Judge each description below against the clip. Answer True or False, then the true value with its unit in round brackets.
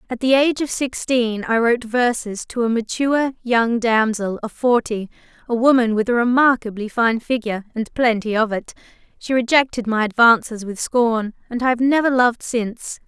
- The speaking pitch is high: True (235 Hz)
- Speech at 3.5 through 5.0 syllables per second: False (5.2 syllables/s)